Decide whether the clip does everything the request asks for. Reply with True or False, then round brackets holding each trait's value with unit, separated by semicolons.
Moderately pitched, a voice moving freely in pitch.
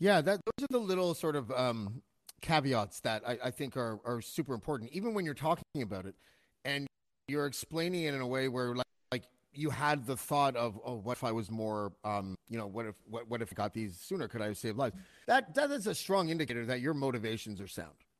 False (125 Hz; 5.7 semitones)